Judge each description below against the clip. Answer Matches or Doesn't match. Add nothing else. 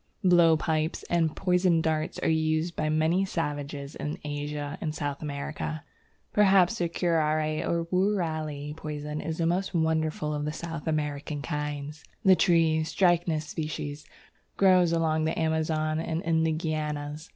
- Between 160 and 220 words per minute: Doesn't match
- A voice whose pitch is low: Doesn't match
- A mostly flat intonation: Matches